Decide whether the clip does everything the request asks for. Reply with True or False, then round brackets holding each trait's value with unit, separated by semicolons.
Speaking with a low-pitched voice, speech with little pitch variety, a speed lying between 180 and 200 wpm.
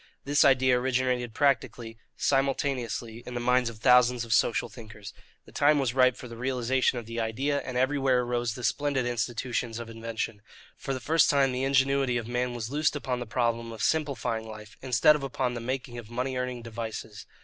True (125 Hz; 2.3 semitones; 195 wpm)